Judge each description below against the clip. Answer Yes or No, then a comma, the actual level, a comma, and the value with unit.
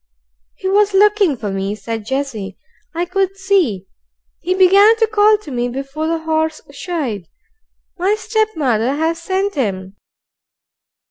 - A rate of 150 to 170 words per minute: No, slow, 135 wpm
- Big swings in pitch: Yes, wide, 8.4 semitones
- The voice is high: Yes, very high, 320 Hz